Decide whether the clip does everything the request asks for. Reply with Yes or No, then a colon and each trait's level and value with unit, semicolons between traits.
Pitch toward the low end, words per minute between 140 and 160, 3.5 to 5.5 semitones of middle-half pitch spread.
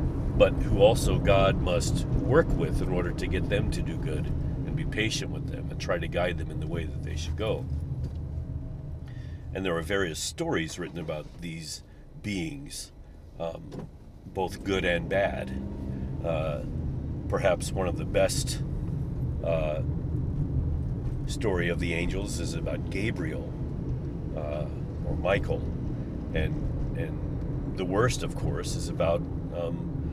Yes: very low, 80 Hz; average, 145 wpm; average, 4.1 semitones